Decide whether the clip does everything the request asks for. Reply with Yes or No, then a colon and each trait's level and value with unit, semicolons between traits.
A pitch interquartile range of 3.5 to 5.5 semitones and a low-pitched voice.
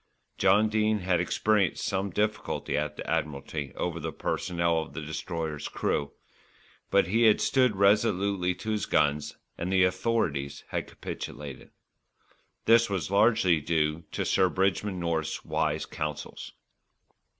Yes: average, 4.7 semitones; very low, 90 Hz